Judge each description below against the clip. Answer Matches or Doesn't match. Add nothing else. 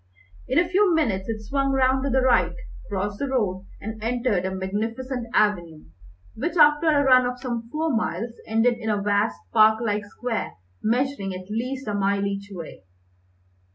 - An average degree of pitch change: Matches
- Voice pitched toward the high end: Matches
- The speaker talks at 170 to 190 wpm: Matches